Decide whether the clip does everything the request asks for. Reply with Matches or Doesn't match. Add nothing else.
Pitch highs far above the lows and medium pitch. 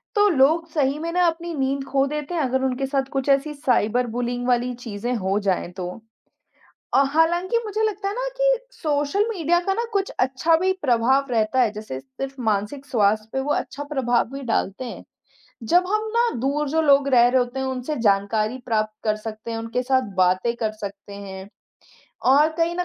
Doesn't match